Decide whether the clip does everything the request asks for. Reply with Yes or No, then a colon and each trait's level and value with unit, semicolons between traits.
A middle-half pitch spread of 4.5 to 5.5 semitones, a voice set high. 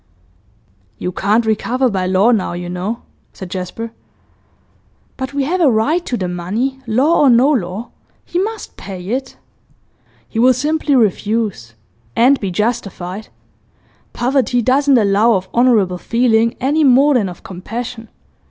Yes: average, 5.2 semitones; high, 230 Hz